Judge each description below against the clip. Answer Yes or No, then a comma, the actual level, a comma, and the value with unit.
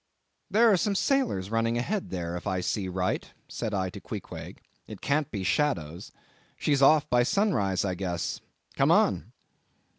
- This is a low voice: Yes, low, 115 Hz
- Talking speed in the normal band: Yes, average, 160 wpm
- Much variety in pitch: Yes, wide, 8.6 semitones